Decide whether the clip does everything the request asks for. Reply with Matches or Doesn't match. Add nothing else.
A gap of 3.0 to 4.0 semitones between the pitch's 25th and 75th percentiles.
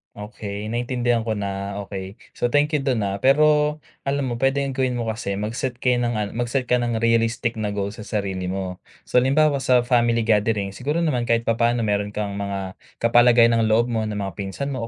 Matches